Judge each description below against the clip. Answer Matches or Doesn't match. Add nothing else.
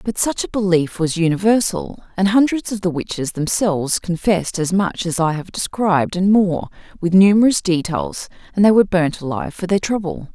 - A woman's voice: Matches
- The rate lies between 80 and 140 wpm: Doesn't match